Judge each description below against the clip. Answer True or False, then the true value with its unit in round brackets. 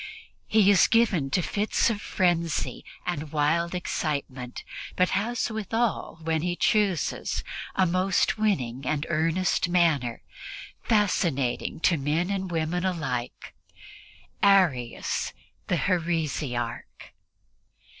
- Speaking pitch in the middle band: True (170 Hz)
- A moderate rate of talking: False (105 wpm)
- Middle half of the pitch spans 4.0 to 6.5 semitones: True (4.3 semitones)